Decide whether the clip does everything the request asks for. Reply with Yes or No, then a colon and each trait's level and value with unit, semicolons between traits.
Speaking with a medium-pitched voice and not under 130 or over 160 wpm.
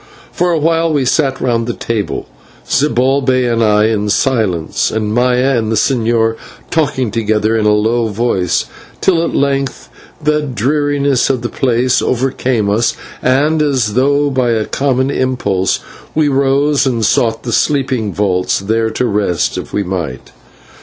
No: low, 125 Hz; average, 155 wpm